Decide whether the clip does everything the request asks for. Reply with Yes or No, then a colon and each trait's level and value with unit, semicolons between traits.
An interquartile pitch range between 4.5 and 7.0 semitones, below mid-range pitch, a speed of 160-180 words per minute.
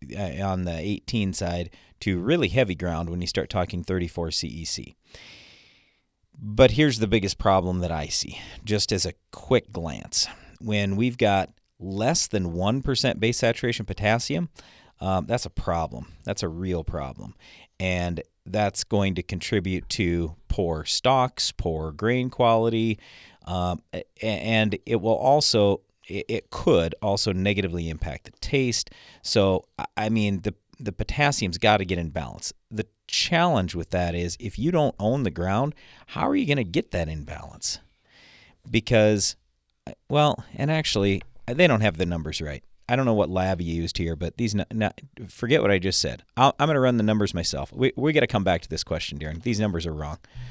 Yes: average, 4.8 semitones; low, 100 Hz; average, 175 wpm